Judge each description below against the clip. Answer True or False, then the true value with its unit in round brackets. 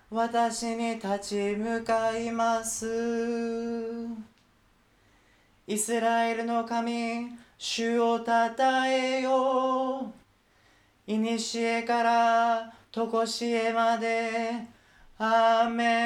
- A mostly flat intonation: True (0.5 semitones)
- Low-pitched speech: False (230 Hz)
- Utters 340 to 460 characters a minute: False (145 characters per minute)